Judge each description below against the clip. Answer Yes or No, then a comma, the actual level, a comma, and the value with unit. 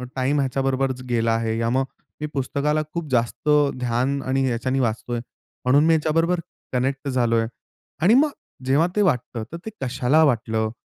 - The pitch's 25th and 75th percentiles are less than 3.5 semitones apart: No, average, 3.8 semitones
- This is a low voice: Yes, low, 130 Hz